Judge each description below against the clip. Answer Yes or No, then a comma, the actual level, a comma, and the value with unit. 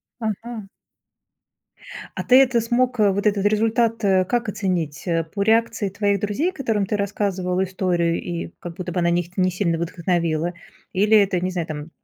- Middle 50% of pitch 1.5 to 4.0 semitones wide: Yes, average, 3.7 semitones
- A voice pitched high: Yes, high, 195 Hz